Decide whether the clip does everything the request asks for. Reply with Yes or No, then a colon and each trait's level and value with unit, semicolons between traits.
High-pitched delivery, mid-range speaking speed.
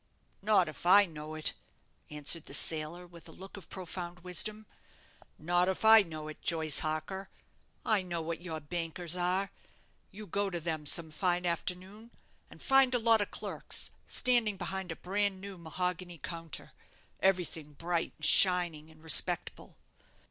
No: medium, 175 Hz; average, 155 wpm